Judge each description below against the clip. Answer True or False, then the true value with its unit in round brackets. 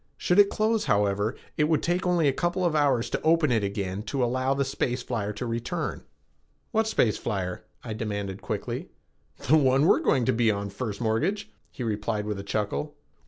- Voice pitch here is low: True (120 Hz)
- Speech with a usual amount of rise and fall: False (6.9 semitones)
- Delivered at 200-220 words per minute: True (205 wpm)